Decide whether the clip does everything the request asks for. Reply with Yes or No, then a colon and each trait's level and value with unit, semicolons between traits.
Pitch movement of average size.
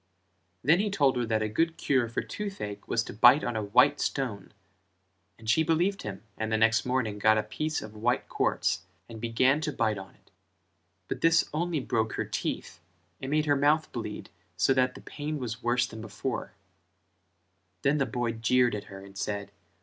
Yes: average, 5.0 semitones